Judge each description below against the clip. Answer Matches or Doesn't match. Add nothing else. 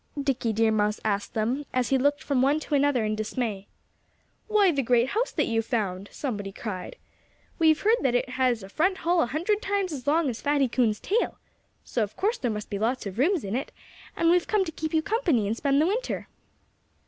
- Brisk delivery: Matches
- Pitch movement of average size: Doesn't match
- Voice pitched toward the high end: Matches